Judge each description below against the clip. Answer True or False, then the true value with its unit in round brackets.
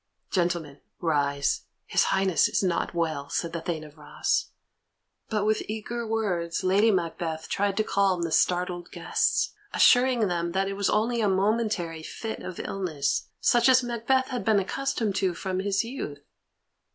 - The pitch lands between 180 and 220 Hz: True (190 Hz)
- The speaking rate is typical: True (160 wpm)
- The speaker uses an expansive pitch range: False (4.5 semitones)